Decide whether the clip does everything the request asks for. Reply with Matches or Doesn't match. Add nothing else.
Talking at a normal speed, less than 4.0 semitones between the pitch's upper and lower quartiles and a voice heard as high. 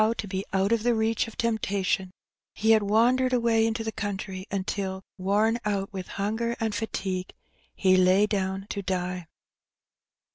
Matches